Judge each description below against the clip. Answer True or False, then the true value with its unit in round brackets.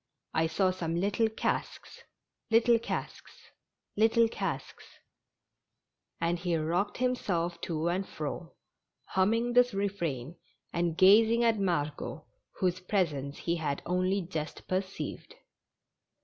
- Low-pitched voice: False (185 Hz)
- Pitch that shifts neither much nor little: True (4.0 semitones)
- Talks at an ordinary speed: False (120 wpm)